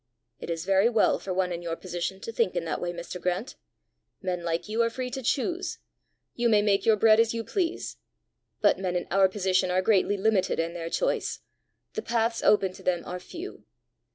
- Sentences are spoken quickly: Yes, fast, 210 wpm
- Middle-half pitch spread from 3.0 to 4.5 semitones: Yes, average, 4.2 semitones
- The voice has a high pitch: Yes, high, 195 Hz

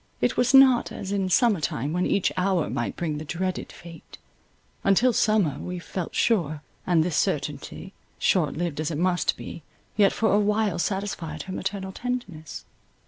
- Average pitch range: Yes, average, 4.2 semitones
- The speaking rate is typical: Yes, average, 160 wpm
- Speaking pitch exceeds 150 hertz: Yes, medium, 185 Hz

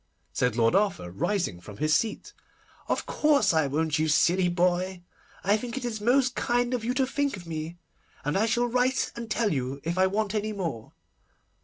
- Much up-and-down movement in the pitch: Yes, wide, 7.0 semitones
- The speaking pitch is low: No, high, 190 Hz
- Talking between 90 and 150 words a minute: No, average, 195 wpm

